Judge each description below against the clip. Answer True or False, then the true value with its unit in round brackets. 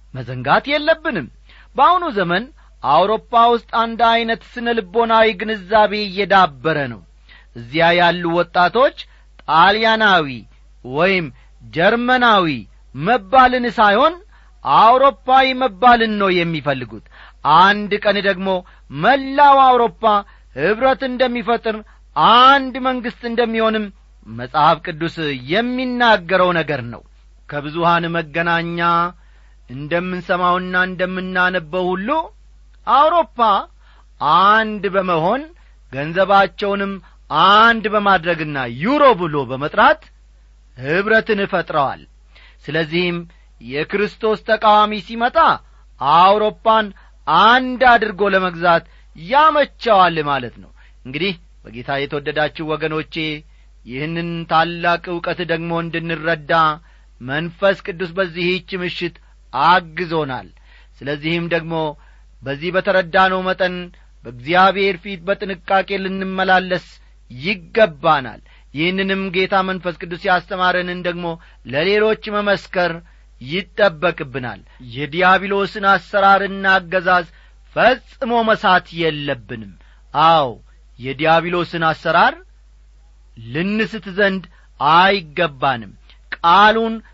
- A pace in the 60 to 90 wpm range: True (80 wpm)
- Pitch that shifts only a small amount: False (5.1 semitones)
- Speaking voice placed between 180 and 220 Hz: True (185 Hz)